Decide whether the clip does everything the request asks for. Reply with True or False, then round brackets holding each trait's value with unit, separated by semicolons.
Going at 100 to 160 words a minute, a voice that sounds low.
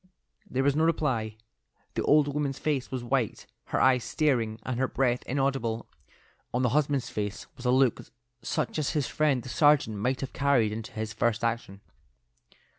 False (175 wpm; 130 Hz)